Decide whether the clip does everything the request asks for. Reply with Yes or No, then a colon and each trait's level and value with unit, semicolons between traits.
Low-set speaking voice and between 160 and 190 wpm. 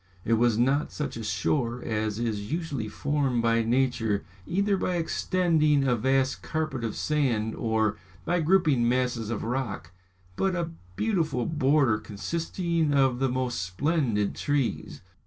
No: low, 130 Hz; average, 140 wpm